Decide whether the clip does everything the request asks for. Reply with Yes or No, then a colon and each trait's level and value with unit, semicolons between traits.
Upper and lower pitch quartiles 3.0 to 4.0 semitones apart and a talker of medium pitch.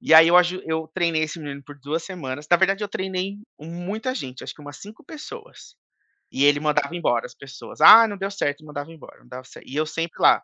No: average, 4.5 semitones; medium, 160 Hz